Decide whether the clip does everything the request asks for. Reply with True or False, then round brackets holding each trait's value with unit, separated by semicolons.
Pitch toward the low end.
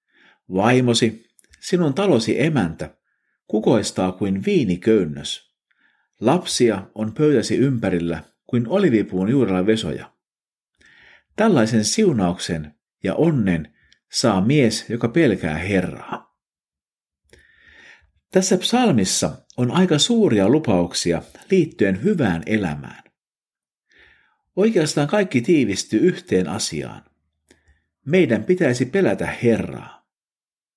True (115 Hz)